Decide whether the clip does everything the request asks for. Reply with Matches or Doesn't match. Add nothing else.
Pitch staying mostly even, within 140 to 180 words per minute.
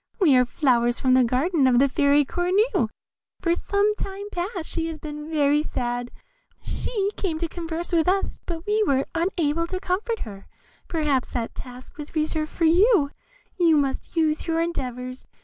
Doesn't match